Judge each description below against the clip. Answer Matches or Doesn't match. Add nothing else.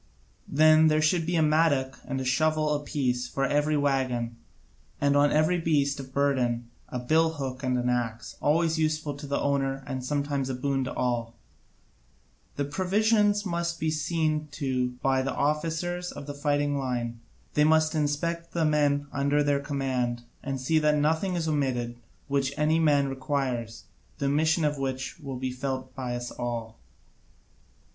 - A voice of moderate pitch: Matches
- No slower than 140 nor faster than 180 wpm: Matches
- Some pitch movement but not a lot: Matches